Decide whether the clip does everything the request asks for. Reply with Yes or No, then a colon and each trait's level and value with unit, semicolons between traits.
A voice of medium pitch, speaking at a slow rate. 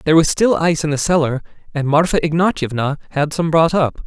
No: medium, 155 Hz; fast, 205 wpm